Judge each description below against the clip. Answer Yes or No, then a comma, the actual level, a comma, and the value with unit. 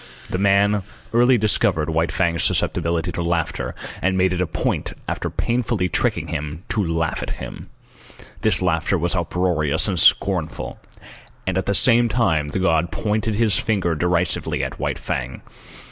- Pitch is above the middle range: No, very low, 90 Hz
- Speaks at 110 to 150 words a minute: No, average, 160 wpm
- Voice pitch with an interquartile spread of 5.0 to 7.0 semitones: No, average, 3.7 semitones